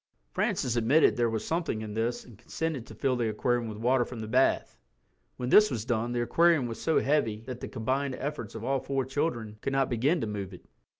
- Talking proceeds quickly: Yes, fast, 230 wpm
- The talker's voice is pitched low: Yes, low, 120 Hz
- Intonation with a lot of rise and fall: No, average, 3.4 semitones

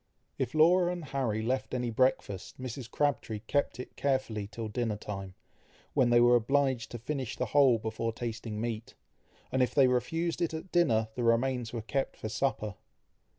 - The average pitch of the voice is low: Yes, low, 120 Hz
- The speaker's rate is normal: Yes, average, 175 wpm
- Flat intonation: No, average, 3.5 semitones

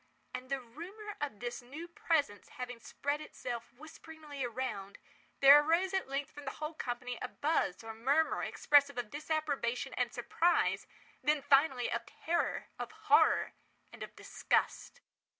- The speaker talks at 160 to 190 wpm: No, average, 145 wpm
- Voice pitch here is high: Yes, very high, 280 Hz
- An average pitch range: Yes, average, 4.3 semitones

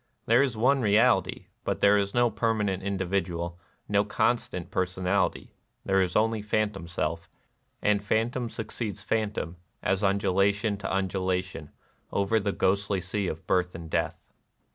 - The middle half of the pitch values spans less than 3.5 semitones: Yes, narrow, 2.6 semitones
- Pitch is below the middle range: Yes, low, 100 Hz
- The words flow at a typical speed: Yes, average, 155 wpm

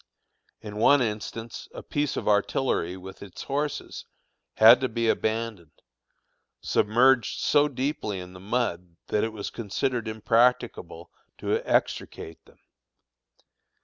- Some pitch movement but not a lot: Yes, average, 3.7 semitones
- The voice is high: No, low, 110 Hz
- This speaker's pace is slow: Yes, slow, 120 wpm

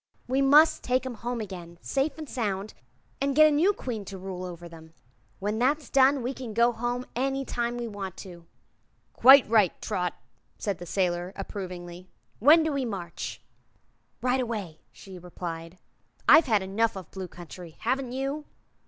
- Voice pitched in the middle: No, high, 220 Hz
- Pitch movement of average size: No, wide, 6.3 semitones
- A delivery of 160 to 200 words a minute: Yes, average, 170 wpm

